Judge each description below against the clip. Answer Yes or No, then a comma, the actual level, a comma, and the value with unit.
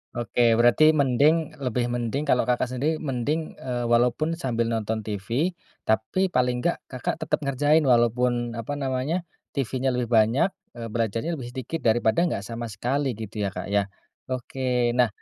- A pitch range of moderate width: Yes, average, 3.2 semitones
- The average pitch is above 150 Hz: No, low, 125 Hz